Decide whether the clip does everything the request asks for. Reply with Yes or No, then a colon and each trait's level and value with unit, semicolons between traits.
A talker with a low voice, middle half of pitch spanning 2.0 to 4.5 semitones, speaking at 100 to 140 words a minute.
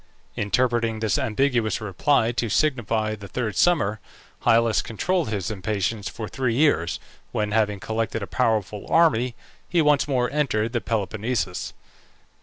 Yes: low, 115 Hz; average, 3.2 semitones; slow, 135 wpm